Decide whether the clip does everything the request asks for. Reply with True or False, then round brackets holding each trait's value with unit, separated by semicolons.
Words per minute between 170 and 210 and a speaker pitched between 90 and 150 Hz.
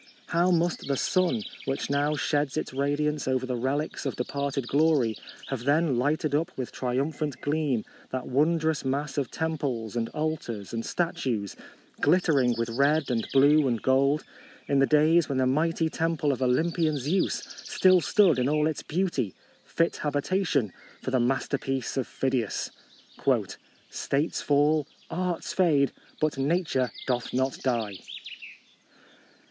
False (150 wpm; 140 Hz)